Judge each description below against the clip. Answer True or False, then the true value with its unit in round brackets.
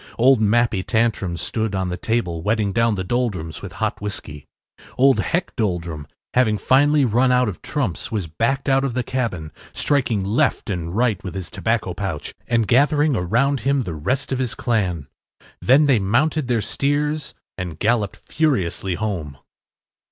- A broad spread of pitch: True (5.8 semitones)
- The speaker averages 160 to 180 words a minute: True (165 wpm)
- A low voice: True (115 Hz)